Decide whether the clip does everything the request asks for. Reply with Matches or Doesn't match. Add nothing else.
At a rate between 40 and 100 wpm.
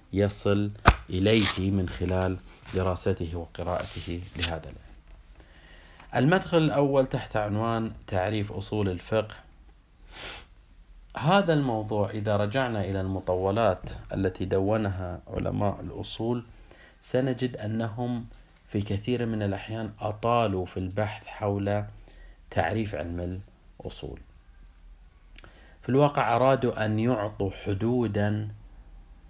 Matches